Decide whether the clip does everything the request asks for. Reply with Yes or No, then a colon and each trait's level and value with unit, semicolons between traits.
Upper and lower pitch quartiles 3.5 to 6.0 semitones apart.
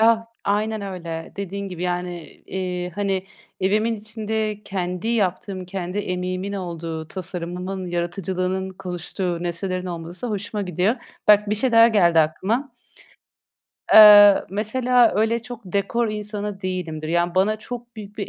No: average, 3.0 semitones